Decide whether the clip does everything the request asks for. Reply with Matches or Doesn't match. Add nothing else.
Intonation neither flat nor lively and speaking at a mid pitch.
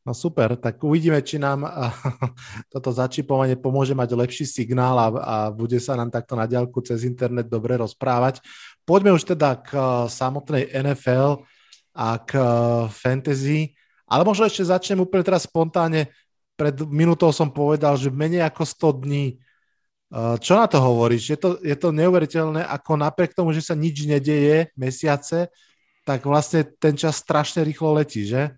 Matches